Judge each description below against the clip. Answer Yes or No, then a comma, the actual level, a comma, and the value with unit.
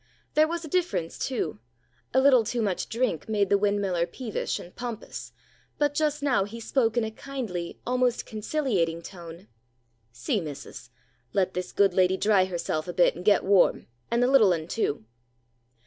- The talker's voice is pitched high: Yes, high, 205 Hz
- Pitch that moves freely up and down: Yes, wide, 6.0 semitones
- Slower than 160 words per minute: No, average, 170 wpm